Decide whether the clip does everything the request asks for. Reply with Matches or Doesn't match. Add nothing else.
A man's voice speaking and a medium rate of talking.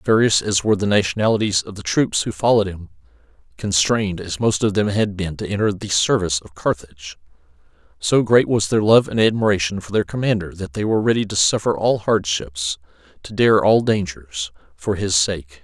Matches